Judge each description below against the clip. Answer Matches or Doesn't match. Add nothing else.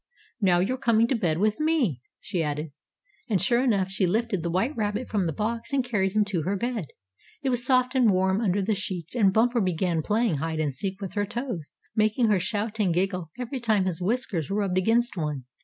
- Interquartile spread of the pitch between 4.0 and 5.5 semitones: Matches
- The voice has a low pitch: Doesn't match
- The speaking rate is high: Matches